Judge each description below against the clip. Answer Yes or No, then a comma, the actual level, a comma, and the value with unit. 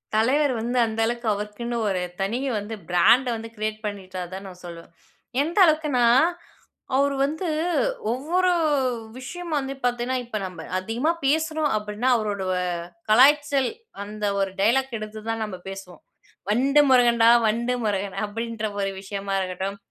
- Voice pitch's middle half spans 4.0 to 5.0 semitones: Yes, average, 4.7 semitones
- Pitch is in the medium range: No, high, 225 Hz